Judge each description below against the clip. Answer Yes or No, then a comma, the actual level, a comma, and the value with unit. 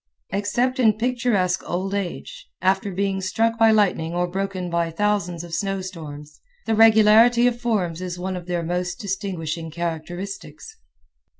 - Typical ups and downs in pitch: Yes, average, 3.5 semitones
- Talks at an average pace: Yes, average, 145 wpm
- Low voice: No, high, 190 Hz